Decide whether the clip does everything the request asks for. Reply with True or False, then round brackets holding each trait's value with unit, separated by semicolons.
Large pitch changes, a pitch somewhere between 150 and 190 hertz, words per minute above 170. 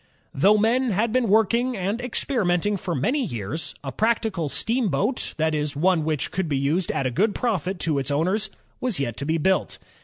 True (6.8 semitones; 185 Hz; 195 wpm)